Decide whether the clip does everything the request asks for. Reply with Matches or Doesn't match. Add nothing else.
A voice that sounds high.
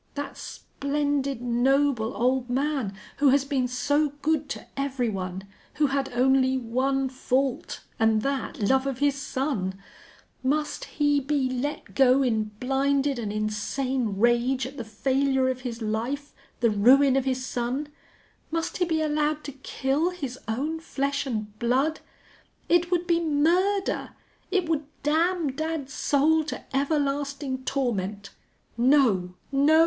Matches